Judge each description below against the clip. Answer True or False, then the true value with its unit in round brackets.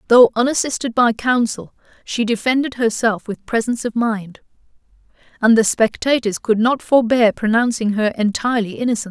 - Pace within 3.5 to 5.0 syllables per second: False (5.2 syllables/s)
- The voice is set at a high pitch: True (230 Hz)